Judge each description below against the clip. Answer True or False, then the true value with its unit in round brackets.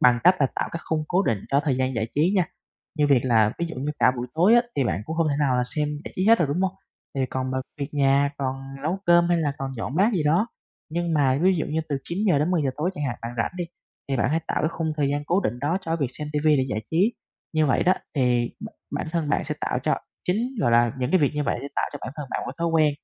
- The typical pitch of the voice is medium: True (150 Hz)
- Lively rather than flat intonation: False (4.4 semitones)